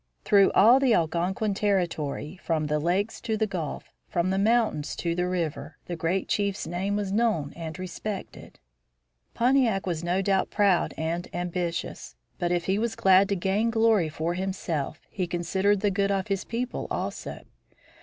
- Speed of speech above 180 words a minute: No, average, 165 wpm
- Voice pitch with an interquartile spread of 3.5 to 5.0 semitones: No, average, 3.1 semitones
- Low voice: No, high, 190 Hz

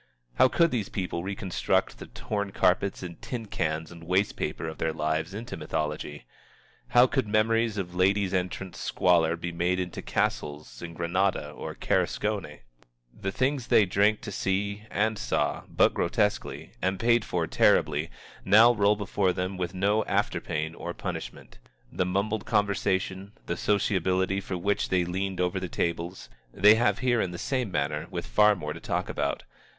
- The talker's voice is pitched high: No, very low, 95 Hz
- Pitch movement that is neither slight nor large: Yes, average, 3.2 semitones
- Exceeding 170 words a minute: No, average, 165 wpm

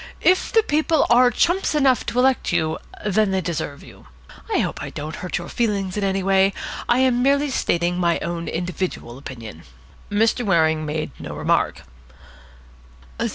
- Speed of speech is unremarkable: Yes, average, 160 wpm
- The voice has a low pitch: No, high, 190 Hz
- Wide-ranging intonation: Yes, wide, 7.0 semitones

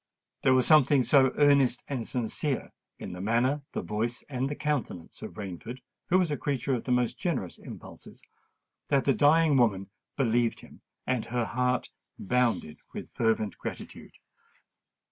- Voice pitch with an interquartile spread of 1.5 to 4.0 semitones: Yes, average, 3.5 semitones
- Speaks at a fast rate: No, average, 155 wpm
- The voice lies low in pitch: Yes, low, 125 Hz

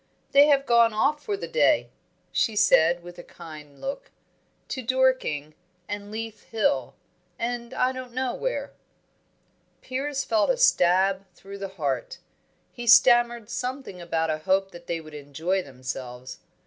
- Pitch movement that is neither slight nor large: No, wide, 7.5 semitones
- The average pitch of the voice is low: No, high, 205 Hz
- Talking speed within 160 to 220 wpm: No, average, 150 wpm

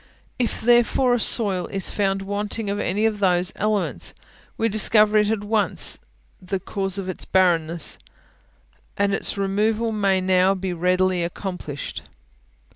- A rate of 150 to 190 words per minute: No, slow, 135 wpm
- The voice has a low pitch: No, high, 195 Hz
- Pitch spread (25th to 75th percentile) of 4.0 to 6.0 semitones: No, narrow, 2.5 semitones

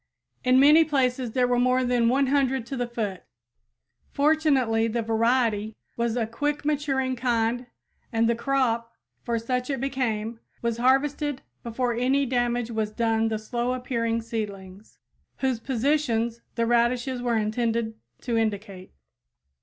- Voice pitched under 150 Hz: No, high, 240 Hz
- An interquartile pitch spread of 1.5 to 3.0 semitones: Yes, narrow, 2.4 semitones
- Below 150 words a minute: Yes, average, 140 wpm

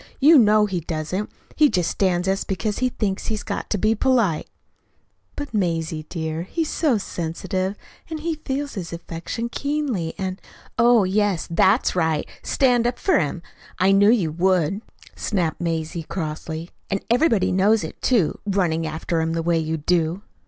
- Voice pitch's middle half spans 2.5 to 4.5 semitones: No, wide, 5.4 semitones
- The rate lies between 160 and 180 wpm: Yes, average, 165 wpm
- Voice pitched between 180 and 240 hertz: Yes, high, 190 Hz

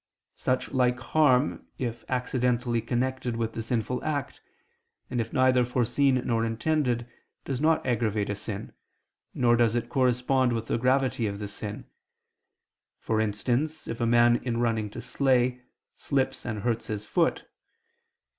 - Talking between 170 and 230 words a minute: No, average, 145 wpm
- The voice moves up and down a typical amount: No, narrow, 2.1 semitones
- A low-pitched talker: Yes, low, 120 Hz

